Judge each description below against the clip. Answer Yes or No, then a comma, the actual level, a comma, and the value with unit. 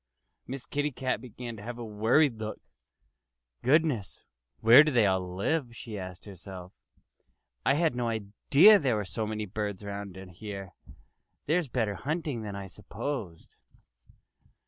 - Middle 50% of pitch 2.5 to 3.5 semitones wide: No, average, 4.9 semitones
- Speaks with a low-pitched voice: Yes, low, 110 Hz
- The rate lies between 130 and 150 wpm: Yes, average, 140 wpm